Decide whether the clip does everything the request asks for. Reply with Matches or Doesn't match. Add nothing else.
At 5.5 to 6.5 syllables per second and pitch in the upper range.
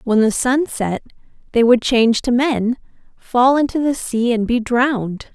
Doesn't match